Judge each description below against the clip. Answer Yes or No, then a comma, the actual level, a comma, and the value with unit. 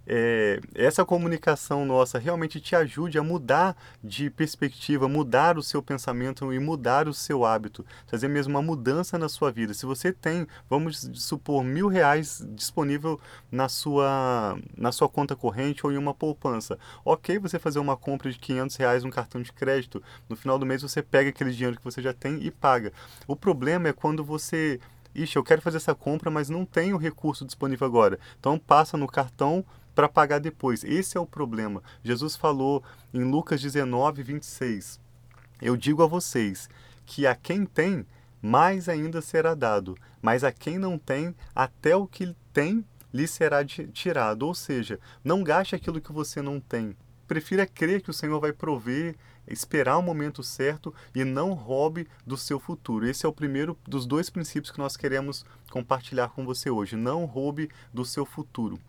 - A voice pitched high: No, medium, 140 Hz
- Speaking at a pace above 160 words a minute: Yes, average, 180 wpm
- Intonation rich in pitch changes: No, average, 4.0 semitones